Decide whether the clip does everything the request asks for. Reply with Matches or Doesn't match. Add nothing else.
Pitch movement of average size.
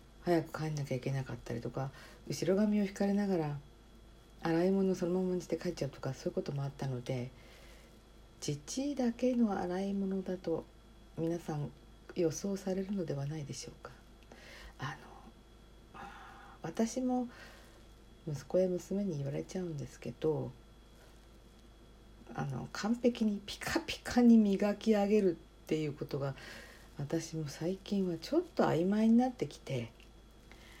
Doesn't match